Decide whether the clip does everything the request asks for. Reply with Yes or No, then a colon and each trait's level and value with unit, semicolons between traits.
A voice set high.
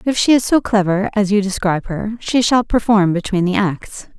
Yes: high, 205 Hz